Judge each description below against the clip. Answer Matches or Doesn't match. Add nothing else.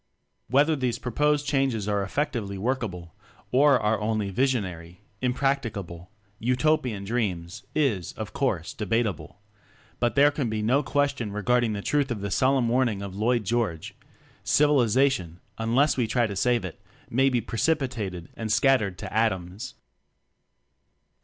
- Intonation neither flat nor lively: Matches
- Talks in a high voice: Doesn't match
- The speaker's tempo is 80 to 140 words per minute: Matches